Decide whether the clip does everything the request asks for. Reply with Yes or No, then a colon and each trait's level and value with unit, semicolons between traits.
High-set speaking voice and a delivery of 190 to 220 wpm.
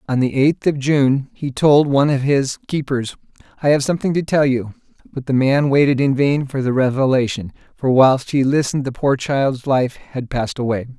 No: low, 135 Hz; average, 200 wpm